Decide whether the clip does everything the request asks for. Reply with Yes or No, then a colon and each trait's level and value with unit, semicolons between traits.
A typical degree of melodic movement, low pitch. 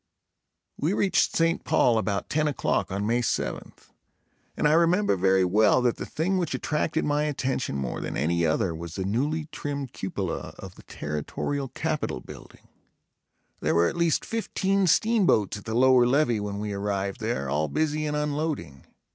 No: wide, 7.8 semitones; low, 125 Hz